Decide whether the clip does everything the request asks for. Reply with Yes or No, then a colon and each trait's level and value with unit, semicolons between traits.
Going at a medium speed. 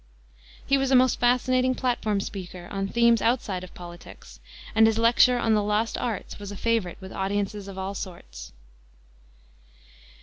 Yes: average, 160 wpm